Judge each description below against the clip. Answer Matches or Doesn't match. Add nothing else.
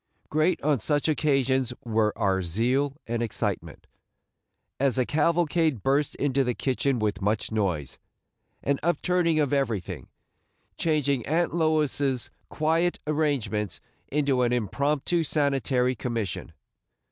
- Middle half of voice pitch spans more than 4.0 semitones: Matches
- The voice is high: Doesn't match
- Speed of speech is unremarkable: Doesn't match